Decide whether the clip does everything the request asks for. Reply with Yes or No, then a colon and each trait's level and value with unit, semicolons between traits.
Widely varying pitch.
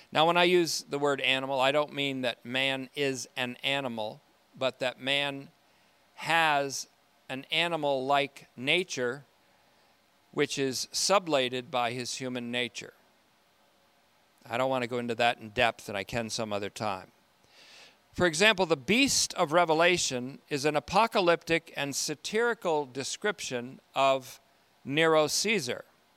No: average, 4.2 semitones